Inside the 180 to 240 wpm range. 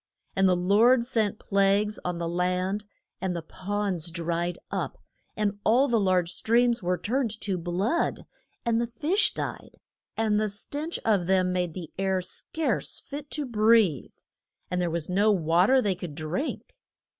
No: average, 165 wpm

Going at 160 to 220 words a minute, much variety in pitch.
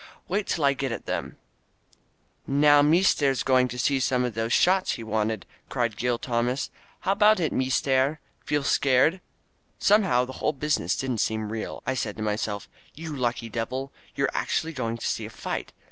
No: average, 180 wpm; average, 4.0 semitones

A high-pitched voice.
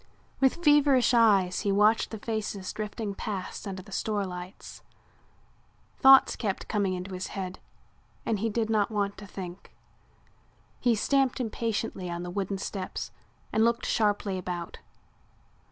Yes: high, 205 Hz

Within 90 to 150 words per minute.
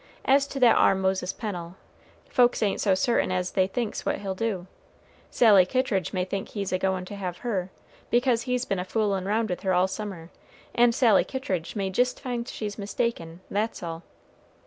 No: average, 190 wpm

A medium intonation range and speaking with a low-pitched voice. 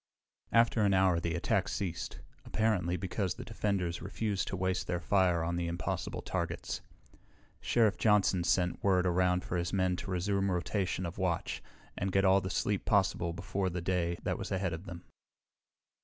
No: narrow, 2.1 semitones; very low, 95 Hz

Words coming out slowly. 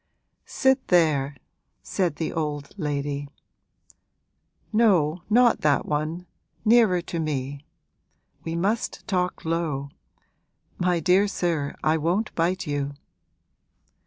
Yes: slow, 100 wpm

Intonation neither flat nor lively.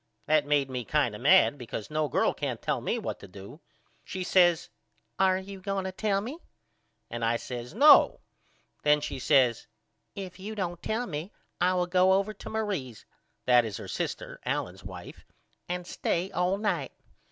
No: wide, 6.4 semitones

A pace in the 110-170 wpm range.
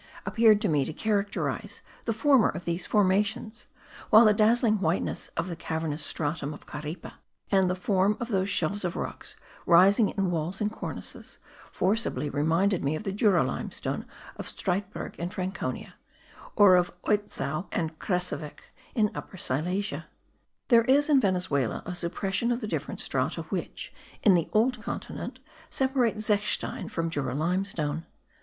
Yes: average, 150 wpm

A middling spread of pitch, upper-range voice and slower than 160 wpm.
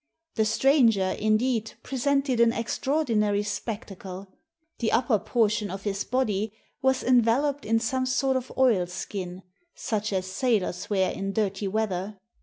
Yes: average, 4.4 semitones; high, 220 Hz; slow, 135 wpm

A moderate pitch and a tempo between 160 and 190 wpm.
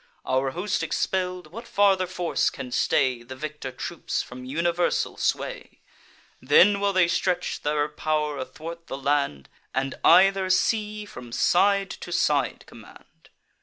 No: medium, 170 Hz; slow, 135 wpm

